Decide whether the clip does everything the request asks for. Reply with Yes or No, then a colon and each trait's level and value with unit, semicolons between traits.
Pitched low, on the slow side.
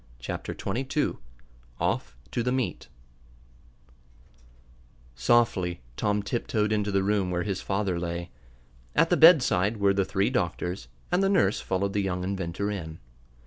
No: low, 100 Hz; average, 145 wpm